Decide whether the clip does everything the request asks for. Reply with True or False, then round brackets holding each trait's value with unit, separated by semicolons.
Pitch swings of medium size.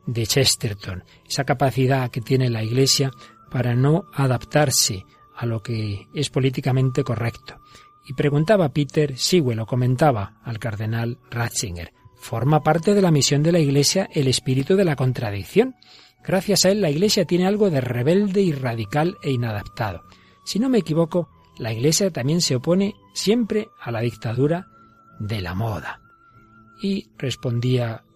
False (6.0 semitones)